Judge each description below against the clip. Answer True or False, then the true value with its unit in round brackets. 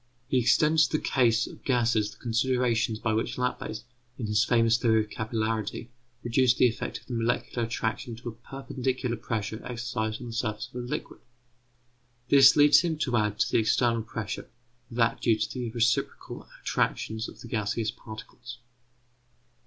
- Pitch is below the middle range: True (115 Hz)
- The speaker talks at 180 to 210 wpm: False (170 wpm)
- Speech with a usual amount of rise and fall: False (2.2 semitones)